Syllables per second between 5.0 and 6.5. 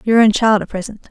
Yes: 5.9 syllables/s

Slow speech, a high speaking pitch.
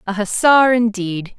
Yes: slow, 130 wpm; high, 215 Hz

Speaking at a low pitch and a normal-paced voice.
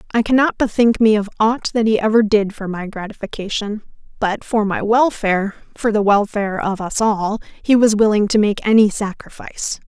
No: high, 210 Hz; average, 170 wpm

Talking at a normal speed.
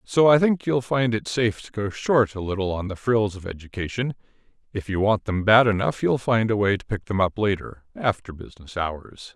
No: fast, 225 wpm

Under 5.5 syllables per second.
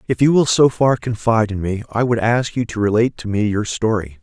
No: 5.8 syllables/s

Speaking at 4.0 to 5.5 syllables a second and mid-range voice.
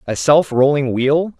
Yes: 4.1 syllables/s; medium, 145 Hz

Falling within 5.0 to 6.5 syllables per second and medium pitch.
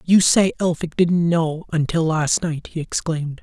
No: 4.4 syllables/s; medium, 165 Hz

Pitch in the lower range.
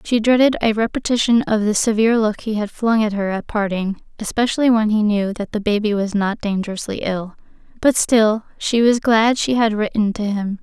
No: high, 215 Hz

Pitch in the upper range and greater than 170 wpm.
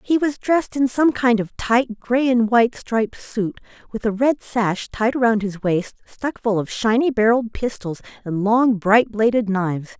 Yes: high, 230 Hz; average, 190 wpm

